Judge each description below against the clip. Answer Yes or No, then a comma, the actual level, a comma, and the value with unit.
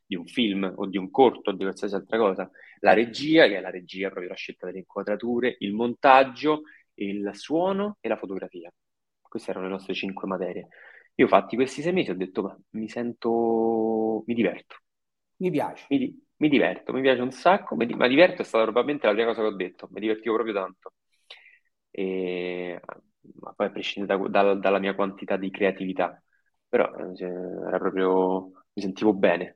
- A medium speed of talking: No, fast, 185 wpm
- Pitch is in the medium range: No, low, 100 Hz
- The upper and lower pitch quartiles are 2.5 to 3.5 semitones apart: No, average, 4.0 semitones